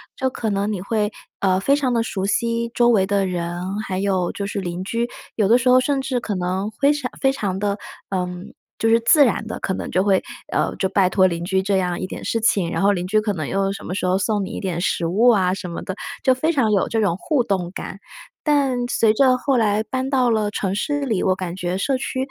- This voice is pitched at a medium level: No, high, 205 Hz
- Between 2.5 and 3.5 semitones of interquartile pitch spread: No, average, 4.5 semitones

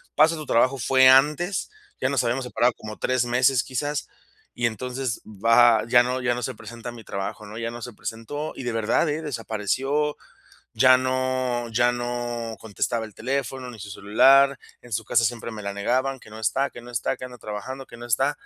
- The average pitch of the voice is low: Yes, low, 120 Hz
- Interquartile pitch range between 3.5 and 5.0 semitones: No, narrow, 2.5 semitones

